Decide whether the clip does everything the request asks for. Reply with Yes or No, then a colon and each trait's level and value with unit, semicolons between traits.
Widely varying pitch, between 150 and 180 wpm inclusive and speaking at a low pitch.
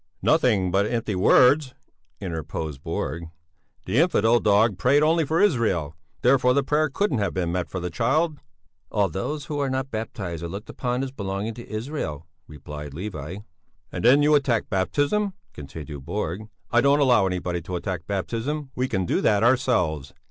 Yes: wide, 7.3 semitones; average, 170 wpm; low, 110 Hz